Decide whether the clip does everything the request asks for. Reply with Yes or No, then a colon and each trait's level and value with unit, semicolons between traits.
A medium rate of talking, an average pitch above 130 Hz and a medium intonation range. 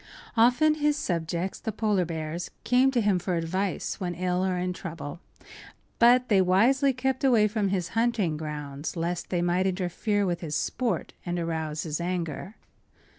Yes: average, 165 wpm; medium, 185 Hz; average, 4.9 semitones